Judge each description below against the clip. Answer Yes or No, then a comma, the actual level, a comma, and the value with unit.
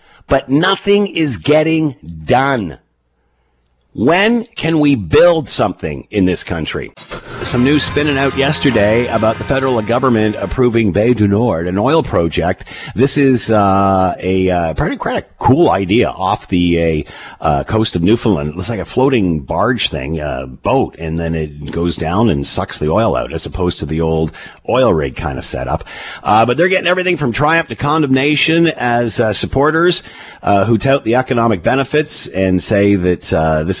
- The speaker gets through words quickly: No, average, 170 wpm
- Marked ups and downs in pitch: Yes, wide, 8.0 semitones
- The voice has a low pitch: Yes, low, 110 Hz